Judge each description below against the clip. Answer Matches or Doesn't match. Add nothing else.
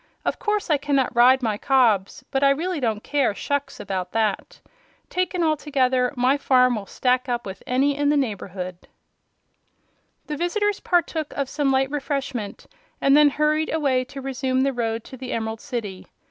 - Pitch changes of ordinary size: Matches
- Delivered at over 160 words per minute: Matches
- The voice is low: Doesn't match